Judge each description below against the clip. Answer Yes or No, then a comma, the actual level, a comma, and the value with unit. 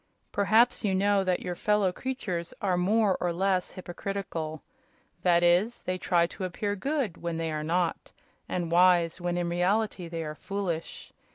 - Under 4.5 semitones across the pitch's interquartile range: Yes, average, 2.7 semitones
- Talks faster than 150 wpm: Yes, average, 165 wpm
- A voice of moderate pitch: Yes, medium, 180 Hz